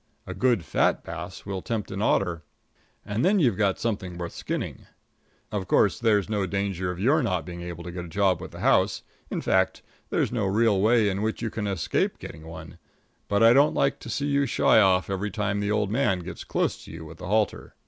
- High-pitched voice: No, low, 100 Hz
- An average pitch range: Yes, average, 3.6 semitones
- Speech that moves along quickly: Yes, fast, 225 wpm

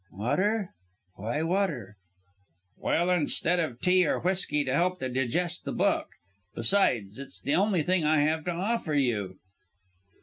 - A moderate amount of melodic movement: No, wide, 6.1 semitones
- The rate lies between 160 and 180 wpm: No, average, 140 wpm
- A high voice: No, medium, 160 Hz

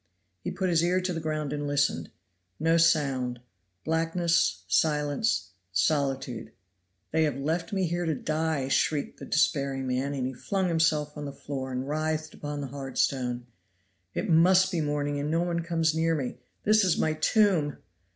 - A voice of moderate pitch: Yes, medium, 155 Hz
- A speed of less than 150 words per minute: No, average, 170 wpm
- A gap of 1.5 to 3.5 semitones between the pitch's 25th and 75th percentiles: Yes, average, 3.1 semitones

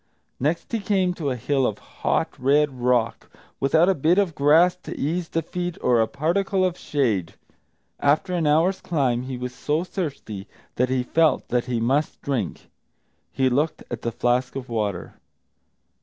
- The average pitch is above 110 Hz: Yes, medium, 140 Hz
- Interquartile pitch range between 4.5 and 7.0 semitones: Yes, average, 5.2 semitones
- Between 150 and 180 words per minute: Yes, average, 170 wpm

